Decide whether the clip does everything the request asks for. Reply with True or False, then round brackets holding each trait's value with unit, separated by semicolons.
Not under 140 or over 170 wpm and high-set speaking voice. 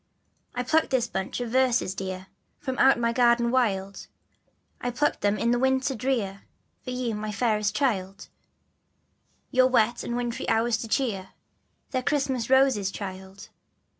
True (150 wpm; 235 Hz)